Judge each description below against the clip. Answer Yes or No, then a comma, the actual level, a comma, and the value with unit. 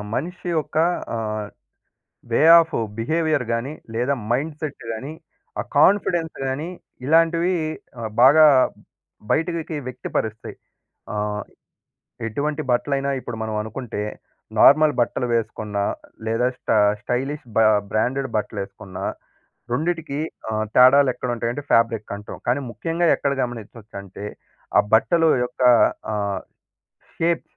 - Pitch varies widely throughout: Yes, wide, 5.8 semitones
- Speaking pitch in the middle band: No, low, 130 Hz